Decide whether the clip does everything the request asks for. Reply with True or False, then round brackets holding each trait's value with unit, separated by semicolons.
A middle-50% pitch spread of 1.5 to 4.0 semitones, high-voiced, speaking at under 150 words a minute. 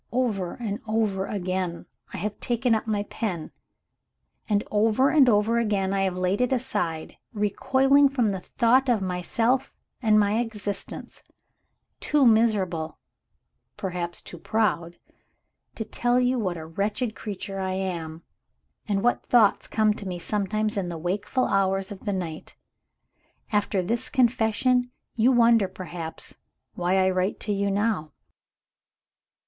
True (3.7 semitones; 205 Hz; 140 wpm)